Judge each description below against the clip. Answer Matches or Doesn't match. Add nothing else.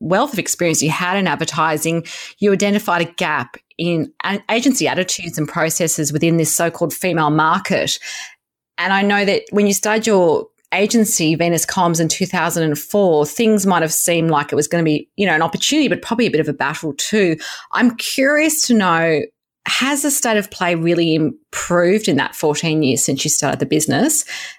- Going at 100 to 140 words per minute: Doesn't match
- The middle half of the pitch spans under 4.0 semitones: Doesn't match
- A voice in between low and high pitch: Matches